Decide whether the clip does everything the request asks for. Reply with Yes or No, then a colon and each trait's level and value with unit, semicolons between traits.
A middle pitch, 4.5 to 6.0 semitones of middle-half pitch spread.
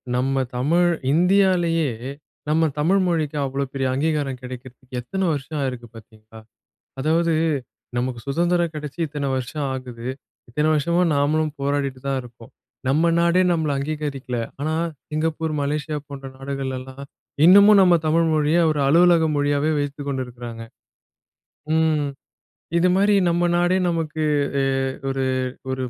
No: medium, 150 Hz; average, 3.7 semitones